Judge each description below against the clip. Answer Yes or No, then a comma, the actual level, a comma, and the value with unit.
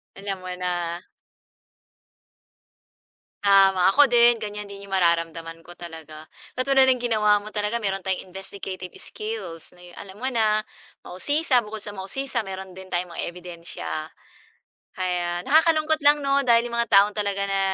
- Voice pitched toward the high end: Yes, high, 195 Hz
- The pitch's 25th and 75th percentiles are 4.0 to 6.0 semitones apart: Yes, average, 4.6 semitones